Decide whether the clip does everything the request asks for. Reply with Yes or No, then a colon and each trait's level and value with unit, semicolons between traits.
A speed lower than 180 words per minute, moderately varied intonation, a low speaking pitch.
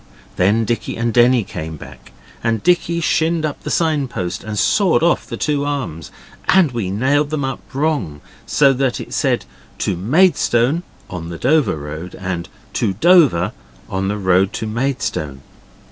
No: average, 160 wpm; wide, 8.0 semitones; low, 120 Hz